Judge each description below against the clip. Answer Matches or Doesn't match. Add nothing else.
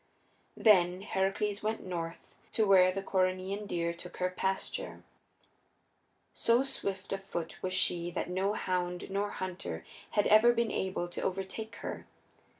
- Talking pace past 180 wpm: Doesn't match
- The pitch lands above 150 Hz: Matches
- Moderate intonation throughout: Doesn't match